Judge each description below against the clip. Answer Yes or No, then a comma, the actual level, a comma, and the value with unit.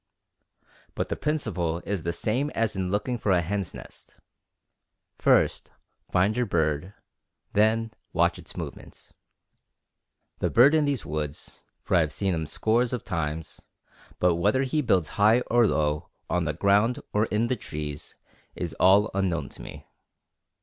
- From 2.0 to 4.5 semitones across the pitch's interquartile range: No, wide, 5.4 semitones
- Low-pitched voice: Yes, low, 100 Hz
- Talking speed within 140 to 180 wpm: Yes, average, 155 wpm